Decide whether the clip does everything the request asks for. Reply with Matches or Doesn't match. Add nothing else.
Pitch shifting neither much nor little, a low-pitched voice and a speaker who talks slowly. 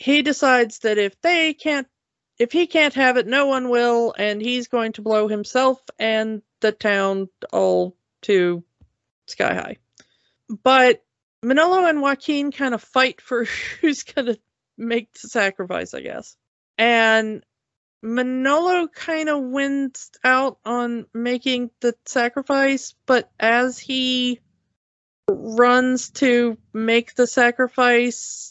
Doesn't match